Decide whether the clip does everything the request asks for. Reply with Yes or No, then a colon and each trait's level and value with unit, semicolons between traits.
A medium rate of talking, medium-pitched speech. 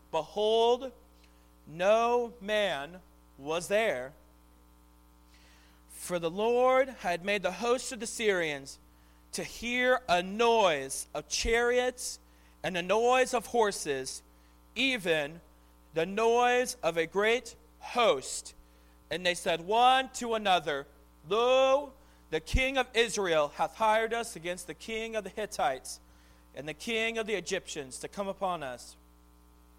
No: slow, 125 wpm; medium, 180 Hz